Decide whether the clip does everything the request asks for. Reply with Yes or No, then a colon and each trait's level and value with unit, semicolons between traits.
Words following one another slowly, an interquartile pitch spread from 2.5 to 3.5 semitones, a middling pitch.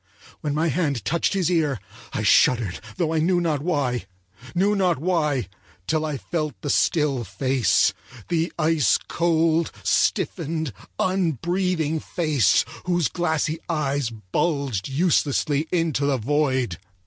No: slow, 125 wpm; average, 3.9 semitones; medium, 155 Hz